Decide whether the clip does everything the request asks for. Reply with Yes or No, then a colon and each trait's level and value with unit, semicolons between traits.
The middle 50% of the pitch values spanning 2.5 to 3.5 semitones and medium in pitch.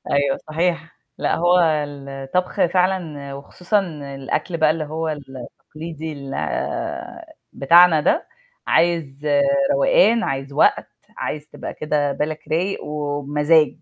Yes: average, 3.2 semitones; medium, 155 Hz